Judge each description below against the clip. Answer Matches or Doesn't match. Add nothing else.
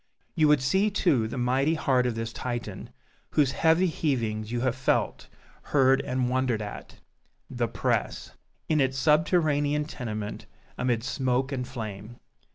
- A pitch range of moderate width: Matches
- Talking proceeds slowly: Doesn't match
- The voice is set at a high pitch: Doesn't match